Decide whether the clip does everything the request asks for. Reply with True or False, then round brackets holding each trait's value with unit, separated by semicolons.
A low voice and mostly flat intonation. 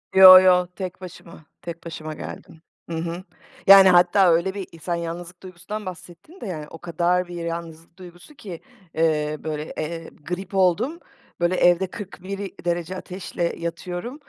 False (175 Hz; 1.9 semitones)